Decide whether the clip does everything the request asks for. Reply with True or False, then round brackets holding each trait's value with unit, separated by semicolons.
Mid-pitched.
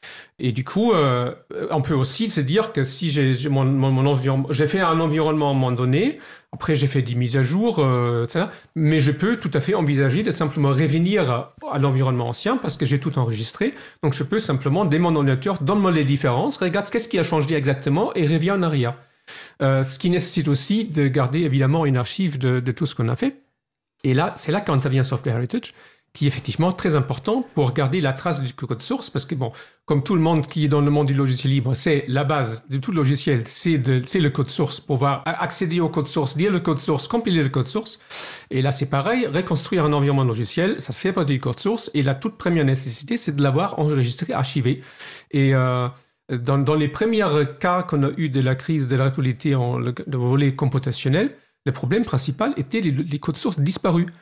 True (145 Hz)